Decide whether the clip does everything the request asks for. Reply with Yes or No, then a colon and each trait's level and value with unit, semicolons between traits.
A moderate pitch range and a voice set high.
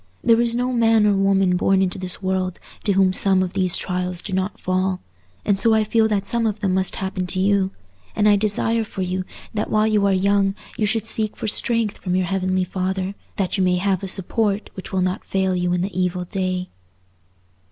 No: narrow, 2.1 semitones; high, 195 Hz